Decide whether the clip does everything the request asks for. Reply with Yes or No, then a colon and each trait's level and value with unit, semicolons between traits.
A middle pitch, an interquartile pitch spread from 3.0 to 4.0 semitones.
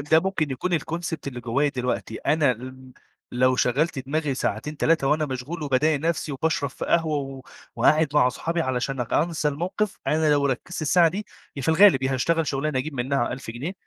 Yes: medium, 145 Hz; average, 3.6 semitones